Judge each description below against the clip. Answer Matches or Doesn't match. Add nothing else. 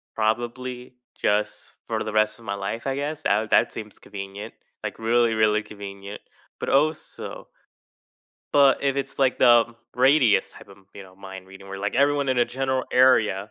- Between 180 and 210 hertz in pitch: Doesn't match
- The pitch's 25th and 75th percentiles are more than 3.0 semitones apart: Matches